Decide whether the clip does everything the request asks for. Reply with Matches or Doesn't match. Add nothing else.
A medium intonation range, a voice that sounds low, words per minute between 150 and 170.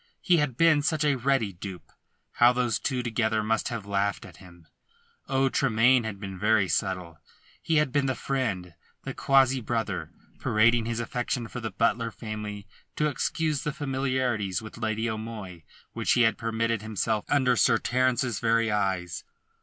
Matches